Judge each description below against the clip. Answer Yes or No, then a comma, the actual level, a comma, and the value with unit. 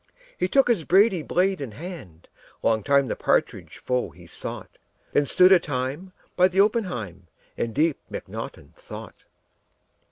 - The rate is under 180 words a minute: Yes, average, 150 wpm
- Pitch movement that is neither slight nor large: No, wide, 6.7 semitones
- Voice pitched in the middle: Yes, medium, 160 Hz